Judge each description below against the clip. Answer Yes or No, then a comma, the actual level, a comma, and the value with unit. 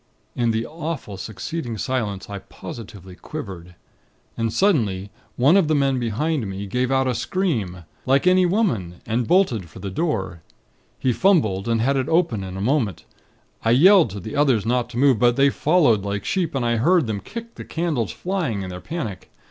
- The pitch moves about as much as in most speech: No, wide, 7.5 semitones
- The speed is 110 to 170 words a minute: No, average, 190 wpm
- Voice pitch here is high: No, low, 120 Hz